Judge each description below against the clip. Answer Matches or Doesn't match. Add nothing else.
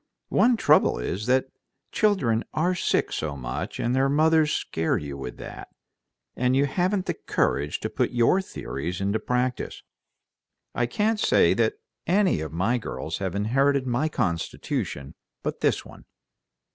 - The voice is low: Matches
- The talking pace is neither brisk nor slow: Matches